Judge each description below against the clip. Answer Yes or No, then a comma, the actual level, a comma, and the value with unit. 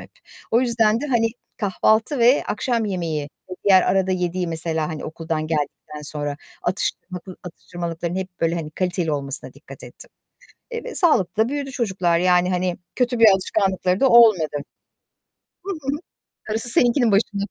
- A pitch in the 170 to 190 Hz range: Yes, medium, 185 Hz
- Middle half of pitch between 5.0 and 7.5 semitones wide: Yes, average, 5.3 semitones